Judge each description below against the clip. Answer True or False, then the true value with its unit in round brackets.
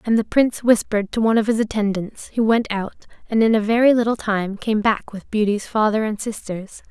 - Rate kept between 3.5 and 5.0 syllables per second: False (5.7 syllables/s)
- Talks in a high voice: True (215 Hz)